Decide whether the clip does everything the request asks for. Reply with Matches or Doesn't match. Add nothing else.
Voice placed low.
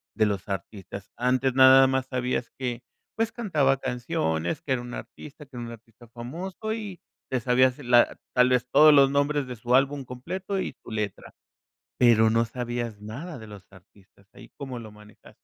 Matches